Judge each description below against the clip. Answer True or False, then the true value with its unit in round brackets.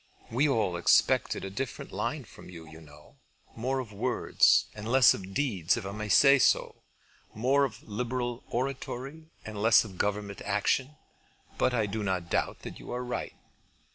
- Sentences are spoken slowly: False (170 wpm)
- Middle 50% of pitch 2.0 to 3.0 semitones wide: False (4.5 semitones)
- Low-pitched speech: True (110 Hz)